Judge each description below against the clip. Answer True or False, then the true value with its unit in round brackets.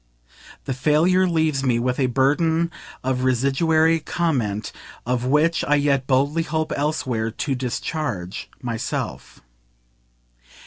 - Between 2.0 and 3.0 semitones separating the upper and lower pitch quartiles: False (4.0 semitones)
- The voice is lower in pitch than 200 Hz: True (140 Hz)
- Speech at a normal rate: False (115 wpm)